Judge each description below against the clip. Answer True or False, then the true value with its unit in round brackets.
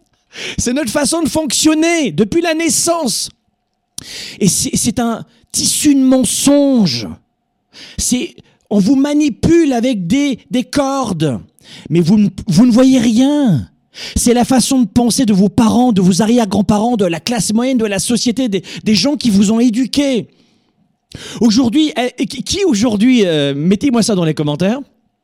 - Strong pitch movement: False (4.5 semitones)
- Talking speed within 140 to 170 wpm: True (150 wpm)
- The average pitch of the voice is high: True (240 Hz)